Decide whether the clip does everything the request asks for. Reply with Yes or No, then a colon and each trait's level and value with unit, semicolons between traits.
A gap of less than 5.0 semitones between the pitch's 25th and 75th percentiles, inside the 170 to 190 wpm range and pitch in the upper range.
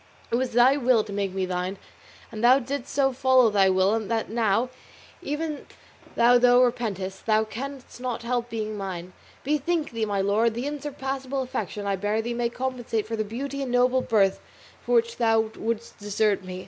Yes: average, 3.8 semitones; average, 185 wpm; high, 235 Hz